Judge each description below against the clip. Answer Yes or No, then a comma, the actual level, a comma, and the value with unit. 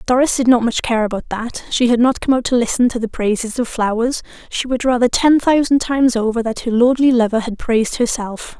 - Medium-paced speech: No, fast, 225 wpm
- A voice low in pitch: No, high, 240 Hz